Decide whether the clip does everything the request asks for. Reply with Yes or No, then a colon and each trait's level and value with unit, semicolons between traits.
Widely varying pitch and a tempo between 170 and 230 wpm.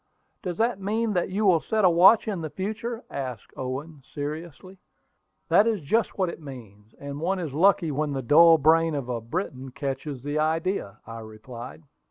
Yes: wide, 5.9 semitones; average, 185 wpm